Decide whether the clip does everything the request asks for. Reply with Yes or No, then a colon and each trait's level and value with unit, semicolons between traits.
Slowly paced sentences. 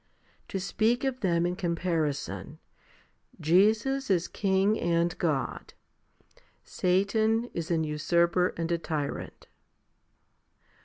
Yes: slow, 105 wpm